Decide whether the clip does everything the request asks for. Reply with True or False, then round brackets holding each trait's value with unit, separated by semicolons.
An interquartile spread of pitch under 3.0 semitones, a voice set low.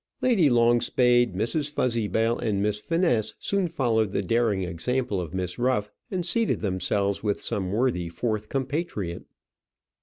False (4.5 semitones; 115 Hz)